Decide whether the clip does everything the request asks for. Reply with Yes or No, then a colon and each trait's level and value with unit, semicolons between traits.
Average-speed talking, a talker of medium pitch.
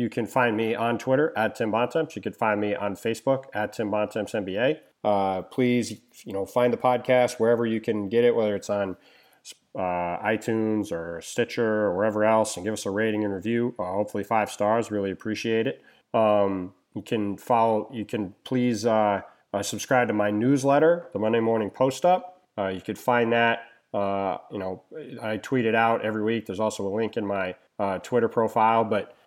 No: average, 195 wpm; low, 110 Hz